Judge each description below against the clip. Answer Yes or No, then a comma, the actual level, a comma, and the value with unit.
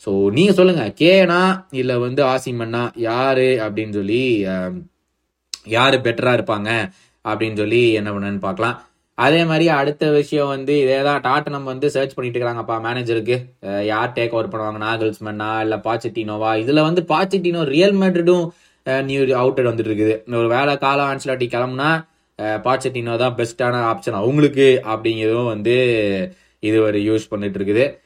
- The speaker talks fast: Yes, fast, 140 wpm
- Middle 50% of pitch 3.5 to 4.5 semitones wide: Yes, average, 4.0 semitones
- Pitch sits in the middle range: No, low, 120 Hz